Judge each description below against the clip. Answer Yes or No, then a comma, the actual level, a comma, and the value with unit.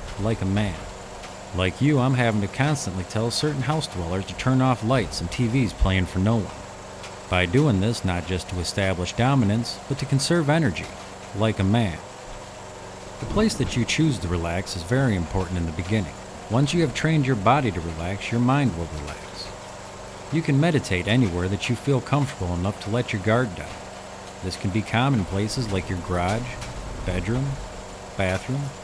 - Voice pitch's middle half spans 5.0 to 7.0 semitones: Yes, wide, 5.4 semitones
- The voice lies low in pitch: Yes, low, 100 Hz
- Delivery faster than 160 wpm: Yes, average, 180 wpm